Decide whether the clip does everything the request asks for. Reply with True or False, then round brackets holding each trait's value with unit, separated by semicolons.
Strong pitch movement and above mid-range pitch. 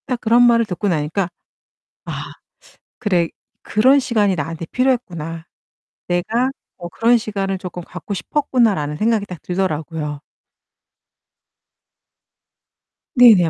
True (5.7 semitones; 195 Hz)